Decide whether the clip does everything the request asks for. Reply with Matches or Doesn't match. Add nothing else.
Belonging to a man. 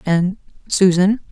Doesn't match